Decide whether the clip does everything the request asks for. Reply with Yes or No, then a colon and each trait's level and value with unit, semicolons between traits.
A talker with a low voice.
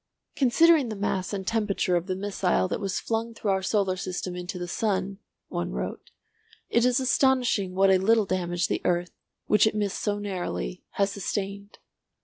No: high, 195 Hz